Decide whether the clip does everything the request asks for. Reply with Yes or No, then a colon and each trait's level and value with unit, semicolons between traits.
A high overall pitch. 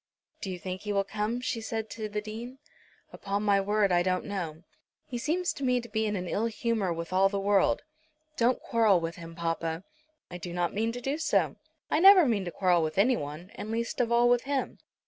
Yes: high, 210 Hz